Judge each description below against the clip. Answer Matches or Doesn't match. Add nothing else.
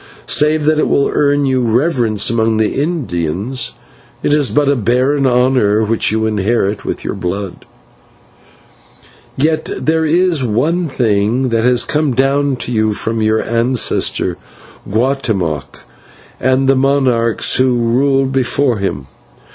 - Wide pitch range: Doesn't match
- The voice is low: Matches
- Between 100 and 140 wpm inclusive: Matches